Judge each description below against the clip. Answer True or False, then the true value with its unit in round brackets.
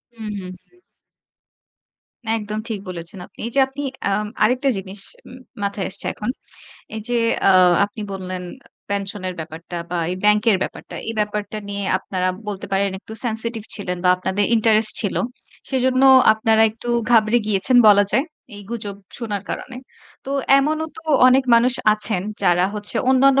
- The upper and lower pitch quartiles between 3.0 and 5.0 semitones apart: True (3.3 semitones)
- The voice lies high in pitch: True (210 Hz)